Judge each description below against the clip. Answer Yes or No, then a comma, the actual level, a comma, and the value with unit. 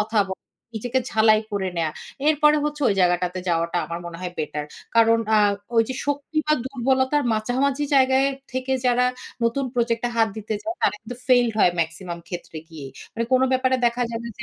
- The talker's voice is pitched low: No, high, 230 Hz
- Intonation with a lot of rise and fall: Yes, wide, 5.8 semitones